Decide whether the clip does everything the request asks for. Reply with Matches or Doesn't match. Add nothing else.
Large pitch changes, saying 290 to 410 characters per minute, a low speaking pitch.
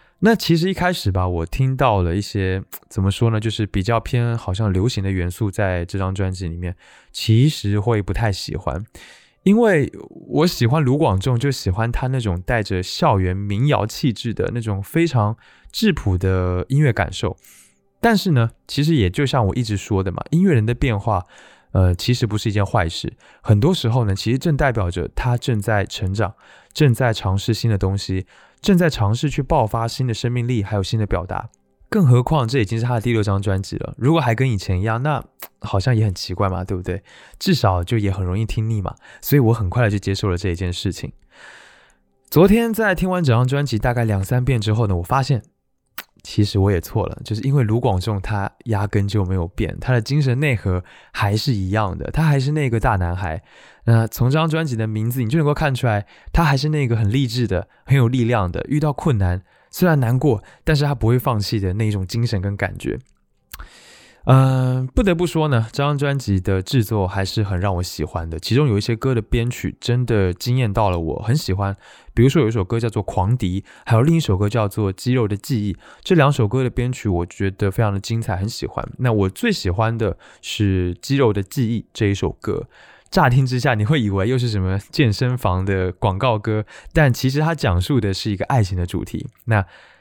Doesn't match